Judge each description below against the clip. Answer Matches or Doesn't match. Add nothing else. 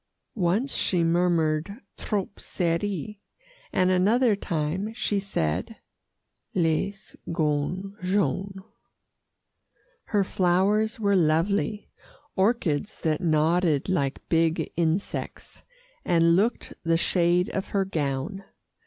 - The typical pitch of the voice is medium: Matches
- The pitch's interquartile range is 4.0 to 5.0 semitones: Doesn't match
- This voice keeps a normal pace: Doesn't match